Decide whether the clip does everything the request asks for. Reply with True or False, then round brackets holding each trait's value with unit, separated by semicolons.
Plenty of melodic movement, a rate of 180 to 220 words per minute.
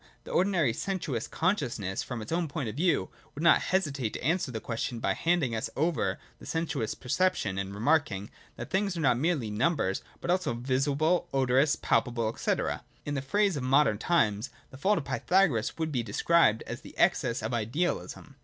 True (6.5 semitones; 190 wpm)